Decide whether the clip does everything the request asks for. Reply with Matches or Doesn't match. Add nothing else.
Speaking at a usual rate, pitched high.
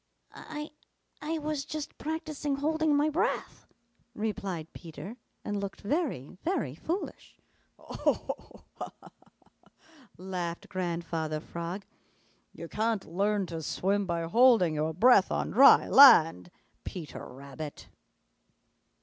Doesn't match